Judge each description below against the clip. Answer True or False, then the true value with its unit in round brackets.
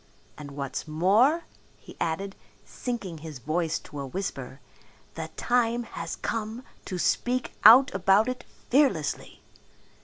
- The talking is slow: True (125 wpm)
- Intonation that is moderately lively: False (7.4 semitones)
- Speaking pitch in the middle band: False (195 Hz)